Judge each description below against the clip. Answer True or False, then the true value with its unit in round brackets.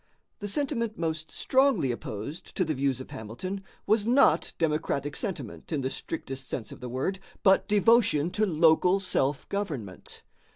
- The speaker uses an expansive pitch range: True (7.0 semitones)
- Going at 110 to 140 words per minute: False (155 wpm)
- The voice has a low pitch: False (165 Hz)